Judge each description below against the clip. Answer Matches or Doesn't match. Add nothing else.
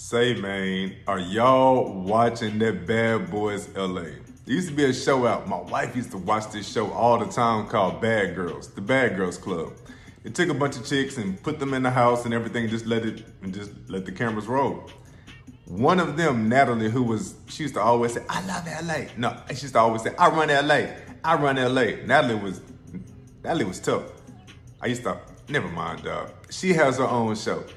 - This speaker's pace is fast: Matches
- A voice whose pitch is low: Matches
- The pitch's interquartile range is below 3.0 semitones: Doesn't match